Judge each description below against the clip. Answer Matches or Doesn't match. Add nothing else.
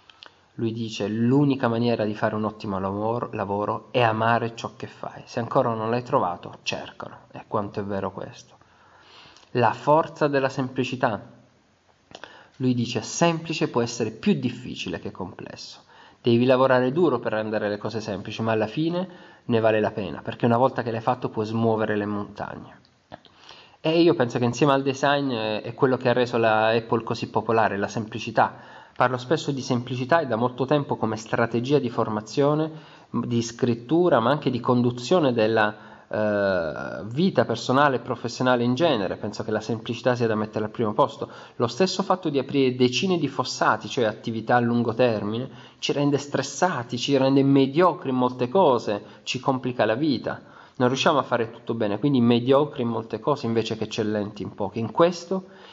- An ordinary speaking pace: Doesn't match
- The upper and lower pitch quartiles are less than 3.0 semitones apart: Doesn't match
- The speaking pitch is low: Matches